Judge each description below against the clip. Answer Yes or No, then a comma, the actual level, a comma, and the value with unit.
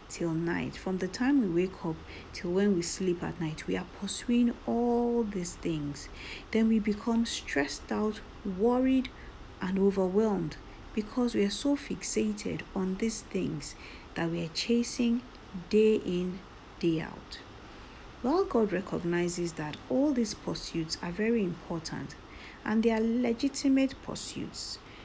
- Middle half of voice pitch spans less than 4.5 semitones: No, average, 5.2 semitones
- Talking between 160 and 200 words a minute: No, average, 140 wpm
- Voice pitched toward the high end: Yes, high, 205 Hz